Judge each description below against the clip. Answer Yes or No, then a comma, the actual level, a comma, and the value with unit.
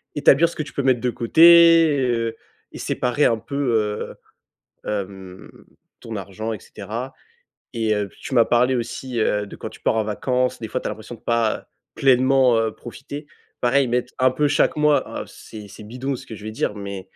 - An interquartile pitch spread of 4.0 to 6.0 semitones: No, average, 3.6 semitones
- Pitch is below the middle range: Yes, low, 120 Hz